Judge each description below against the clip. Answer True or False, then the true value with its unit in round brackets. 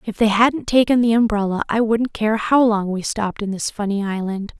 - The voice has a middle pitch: False (215 Hz)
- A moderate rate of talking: False (220 wpm)